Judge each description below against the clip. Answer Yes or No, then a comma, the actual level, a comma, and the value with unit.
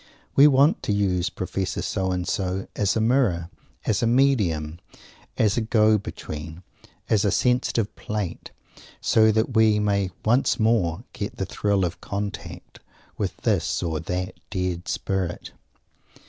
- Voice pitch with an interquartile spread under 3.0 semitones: No, average, 3.5 semitones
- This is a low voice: Yes, low, 100 Hz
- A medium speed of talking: Yes, average, 145 wpm